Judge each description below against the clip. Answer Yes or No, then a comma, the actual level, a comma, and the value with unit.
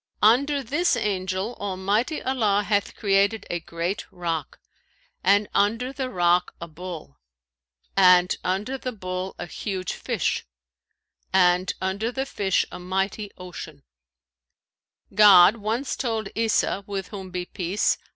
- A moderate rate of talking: No, slow, 125 wpm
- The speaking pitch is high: Yes, high, 195 Hz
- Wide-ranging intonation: No, average, 3.4 semitones